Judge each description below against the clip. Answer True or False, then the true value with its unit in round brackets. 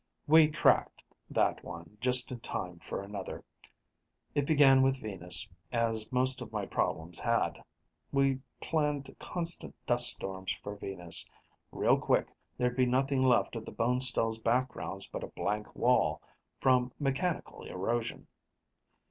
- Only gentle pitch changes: False (4.1 semitones)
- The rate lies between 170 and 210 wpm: False (135 wpm)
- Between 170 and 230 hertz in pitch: False (125 Hz)